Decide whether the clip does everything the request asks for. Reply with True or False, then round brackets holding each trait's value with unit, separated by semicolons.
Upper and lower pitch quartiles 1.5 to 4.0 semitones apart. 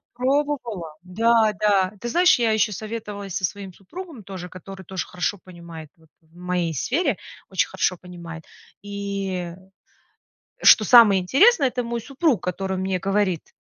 False (4.5 semitones)